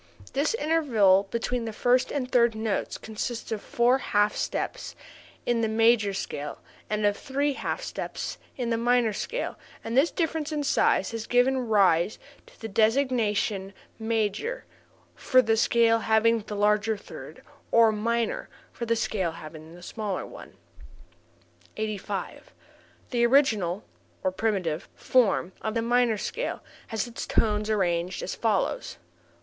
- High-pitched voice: Yes, high, 225 Hz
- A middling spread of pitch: Yes, average, 3.0 semitones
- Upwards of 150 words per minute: No, average, 145 wpm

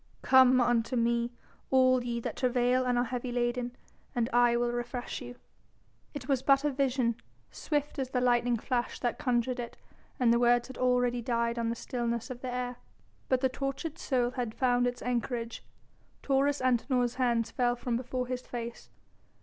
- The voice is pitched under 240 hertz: No, high, 245 Hz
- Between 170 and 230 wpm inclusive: Yes, average, 175 wpm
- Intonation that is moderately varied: No, narrow, 1.2 semitones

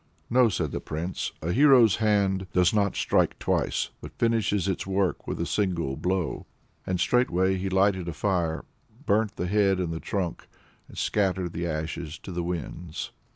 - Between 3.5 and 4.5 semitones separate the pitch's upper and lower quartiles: No, average, 2.9 semitones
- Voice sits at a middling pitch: No, very low, 95 Hz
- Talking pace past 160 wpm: Yes, average, 170 wpm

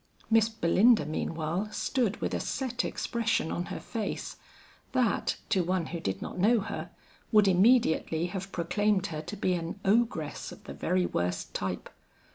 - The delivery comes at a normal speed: Yes, average, 160 wpm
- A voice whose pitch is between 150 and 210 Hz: Yes, high, 190 Hz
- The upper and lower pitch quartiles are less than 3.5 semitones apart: No, average, 5.0 semitones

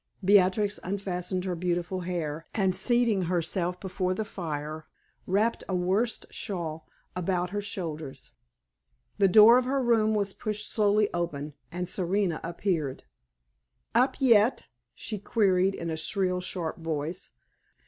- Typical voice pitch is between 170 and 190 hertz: Yes, medium, 185 Hz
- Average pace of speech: No, slow, 130 wpm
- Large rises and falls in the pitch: No, average, 3.2 semitones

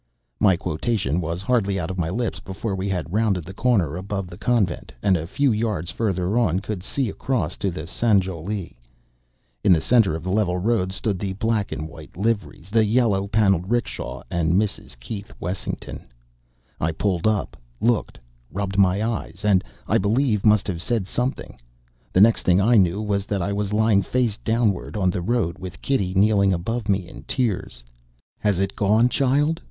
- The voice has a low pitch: Yes, low, 100 Hz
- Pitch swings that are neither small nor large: Yes, average, 3.5 semitones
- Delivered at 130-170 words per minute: No, average, 180 wpm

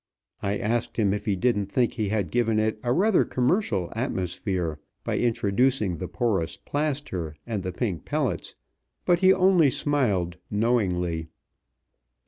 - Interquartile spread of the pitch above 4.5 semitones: Yes, wide, 5.4 semitones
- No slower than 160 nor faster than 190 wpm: No, average, 140 wpm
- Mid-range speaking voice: No, low, 110 Hz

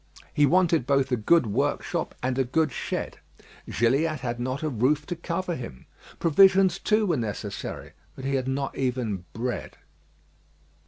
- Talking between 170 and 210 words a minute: No, average, 155 wpm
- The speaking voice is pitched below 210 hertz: Yes, low, 135 Hz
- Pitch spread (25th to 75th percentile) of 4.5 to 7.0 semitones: Yes, average, 5.0 semitones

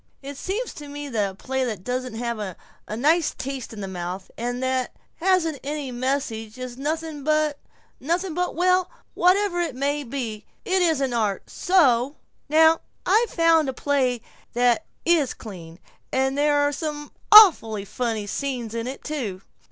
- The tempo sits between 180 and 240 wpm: No, average, 160 wpm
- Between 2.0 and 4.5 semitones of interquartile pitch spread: No, average, 5.1 semitones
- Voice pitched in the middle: No, very high, 275 Hz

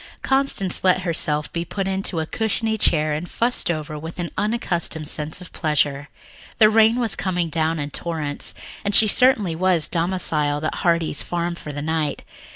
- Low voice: No, medium, 170 Hz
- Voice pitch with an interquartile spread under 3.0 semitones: No, average, 4.0 semitones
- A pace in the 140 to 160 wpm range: No, average, 170 wpm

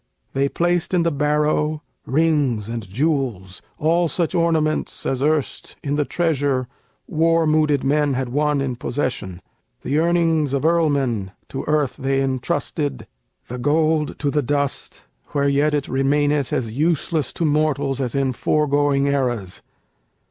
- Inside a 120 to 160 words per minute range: Yes, average, 140 wpm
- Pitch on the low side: No, medium, 145 Hz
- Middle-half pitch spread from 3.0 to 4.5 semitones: No, narrow, 2.5 semitones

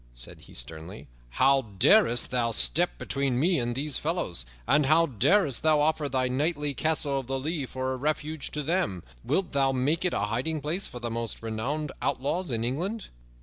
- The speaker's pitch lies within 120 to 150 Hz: Yes, medium, 140 Hz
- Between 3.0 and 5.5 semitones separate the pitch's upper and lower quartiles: Yes, average, 4.5 semitones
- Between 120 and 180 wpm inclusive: No, average, 190 wpm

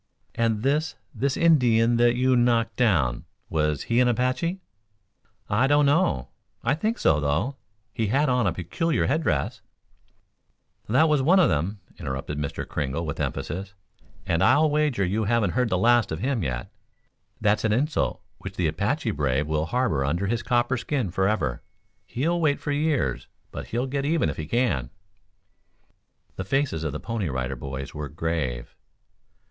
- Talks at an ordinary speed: Yes, average, 165 wpm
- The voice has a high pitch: No, low, 115 Hz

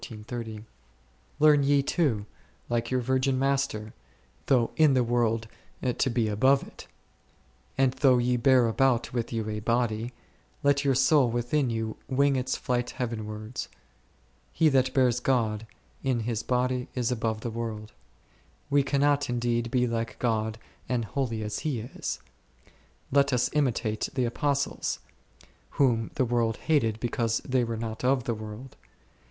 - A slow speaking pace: No, average, 145 wpm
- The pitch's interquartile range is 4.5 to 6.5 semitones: No, average, 2.8 semitones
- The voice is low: Yes, low, 125 Hz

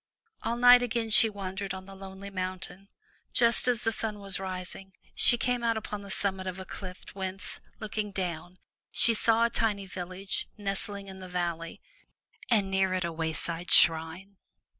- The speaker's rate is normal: Yes, average, 170 wpm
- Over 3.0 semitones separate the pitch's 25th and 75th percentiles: No, narrow, 2.6 semitones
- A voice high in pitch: Yes, high, 195 Hz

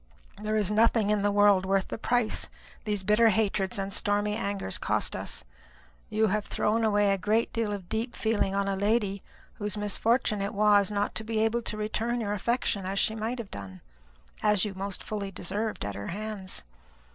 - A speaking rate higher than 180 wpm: Yes, average, 190 wpm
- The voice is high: Yes, high, 210 Hz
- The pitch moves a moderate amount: No, narrow, 1.8 semitones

